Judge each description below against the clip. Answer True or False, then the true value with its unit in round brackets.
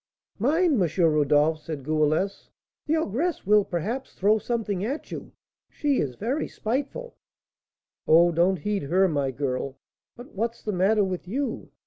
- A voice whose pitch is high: True (195 Hz)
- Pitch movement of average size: False (7.2 semitones)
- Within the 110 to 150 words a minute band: True (145 wpm)